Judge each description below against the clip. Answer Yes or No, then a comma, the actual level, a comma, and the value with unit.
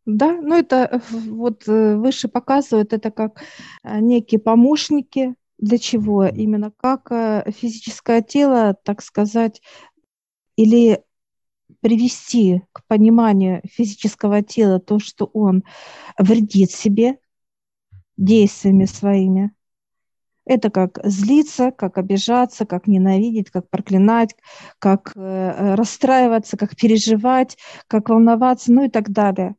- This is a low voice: No, high, 220 Hz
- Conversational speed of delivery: No, slow, 100 wpm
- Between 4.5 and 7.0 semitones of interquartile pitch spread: No, average, 3.1 semitones